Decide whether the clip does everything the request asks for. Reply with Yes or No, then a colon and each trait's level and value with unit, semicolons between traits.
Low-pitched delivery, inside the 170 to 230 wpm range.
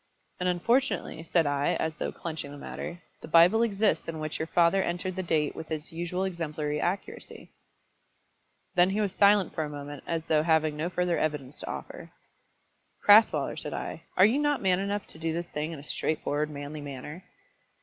No: medium, 165 Hz; average, 190 wpm